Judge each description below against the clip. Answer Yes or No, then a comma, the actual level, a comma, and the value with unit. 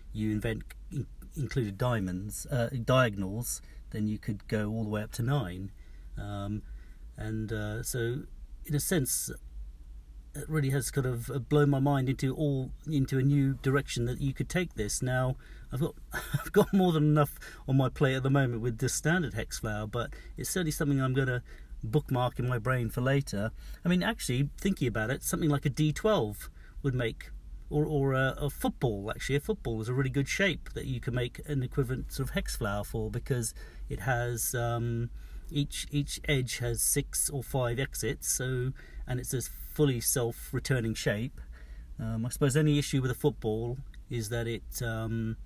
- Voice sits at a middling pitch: No, low, 125 Hz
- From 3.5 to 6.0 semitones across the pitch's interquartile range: Yes, average, 4.1 semitones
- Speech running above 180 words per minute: Yes, average, 190 wpm